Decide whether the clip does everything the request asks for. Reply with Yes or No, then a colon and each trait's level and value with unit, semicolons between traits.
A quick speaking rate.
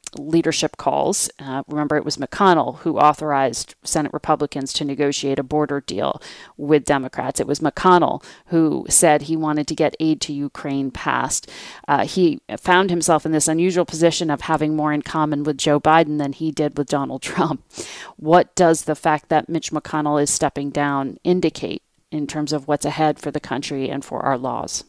No: average, 185 wpm